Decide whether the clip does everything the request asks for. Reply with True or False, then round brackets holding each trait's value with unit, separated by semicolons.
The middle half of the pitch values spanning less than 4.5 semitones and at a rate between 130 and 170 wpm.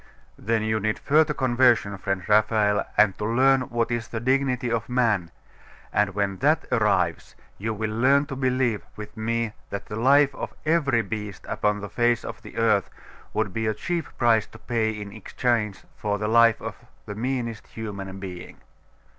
False (2.9 semitones; 180 wpm)